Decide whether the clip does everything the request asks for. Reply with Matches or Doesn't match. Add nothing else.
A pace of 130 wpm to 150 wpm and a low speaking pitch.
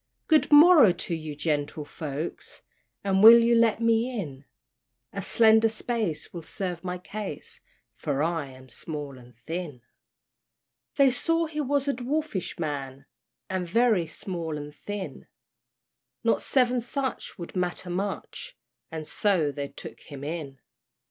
Doesn't match